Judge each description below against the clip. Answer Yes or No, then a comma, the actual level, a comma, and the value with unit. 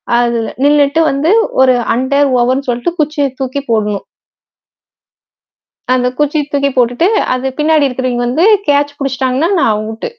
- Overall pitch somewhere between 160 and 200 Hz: No, very high, 270 Hz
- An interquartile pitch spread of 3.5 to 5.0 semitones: No, average, 3.0 semitones